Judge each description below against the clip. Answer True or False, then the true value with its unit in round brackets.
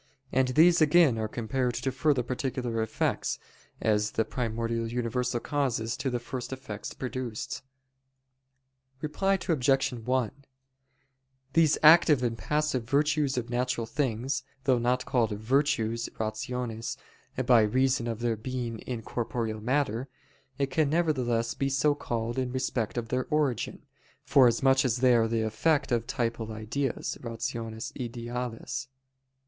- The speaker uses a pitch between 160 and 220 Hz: False (125 Hz)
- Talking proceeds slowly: True (130 wpm)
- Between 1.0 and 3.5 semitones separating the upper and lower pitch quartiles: True (2.7 semitones)